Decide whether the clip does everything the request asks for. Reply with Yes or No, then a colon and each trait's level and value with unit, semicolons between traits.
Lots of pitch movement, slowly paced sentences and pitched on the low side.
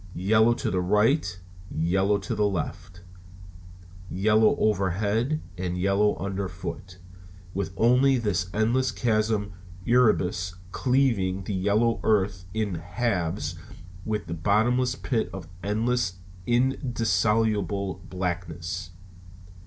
No: average, 3.6 semitones; slow, 110 wpm; low, 100 Hz